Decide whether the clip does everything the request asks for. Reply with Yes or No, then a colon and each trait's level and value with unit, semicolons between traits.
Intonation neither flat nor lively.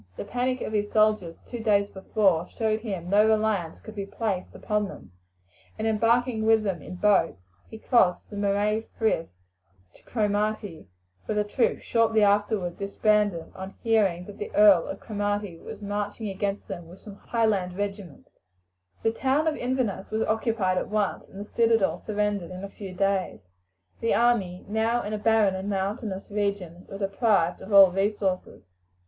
No: narrow, 2.2 semitones